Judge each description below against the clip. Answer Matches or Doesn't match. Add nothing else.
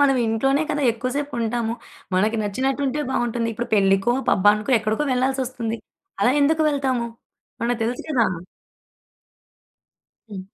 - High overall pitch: Matches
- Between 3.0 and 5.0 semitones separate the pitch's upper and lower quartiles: Matches